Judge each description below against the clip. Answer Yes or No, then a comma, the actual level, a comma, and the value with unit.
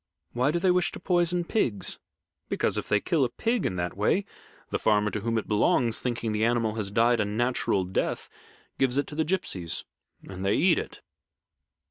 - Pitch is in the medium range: No, low, 115 Hz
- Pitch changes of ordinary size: No, wide, 7.4 semitones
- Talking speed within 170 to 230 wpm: Yes, average, 195 wpm